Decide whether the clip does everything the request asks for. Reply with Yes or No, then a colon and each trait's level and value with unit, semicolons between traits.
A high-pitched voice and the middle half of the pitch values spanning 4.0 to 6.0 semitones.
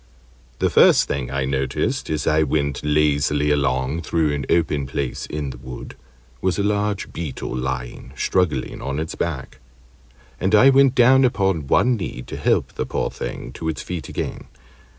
No: very low, 75 Hz; average, 5.3 semitones